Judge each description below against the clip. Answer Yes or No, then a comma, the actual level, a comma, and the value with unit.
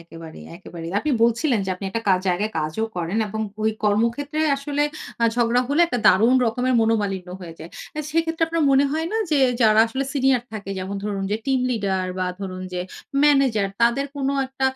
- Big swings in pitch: Yes, wide, 5.9 semitones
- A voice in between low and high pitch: No, high, 225 Hz